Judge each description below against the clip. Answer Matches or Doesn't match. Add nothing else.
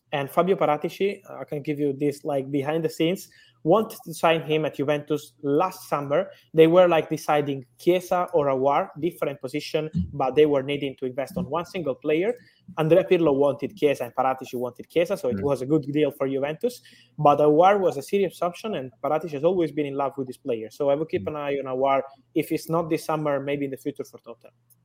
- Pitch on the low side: Doesn't match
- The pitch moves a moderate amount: Matches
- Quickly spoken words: Matches